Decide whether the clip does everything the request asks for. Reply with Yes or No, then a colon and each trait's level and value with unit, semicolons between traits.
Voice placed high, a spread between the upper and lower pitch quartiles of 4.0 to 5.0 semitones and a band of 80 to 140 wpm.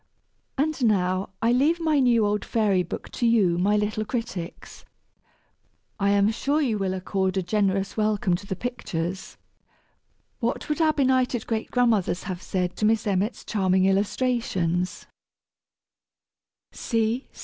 Yes: high, 210 Hz; average, 4.3 semitones; slow, 135 wpm